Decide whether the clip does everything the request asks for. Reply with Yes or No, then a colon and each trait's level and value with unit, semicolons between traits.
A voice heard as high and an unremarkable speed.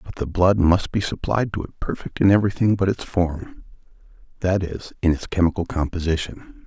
No: very low, 90 Hz; average, 170 wpm